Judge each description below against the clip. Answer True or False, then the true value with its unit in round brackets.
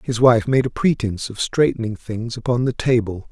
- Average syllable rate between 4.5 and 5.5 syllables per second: True (5.3 syllables/s)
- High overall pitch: False (115 Hz)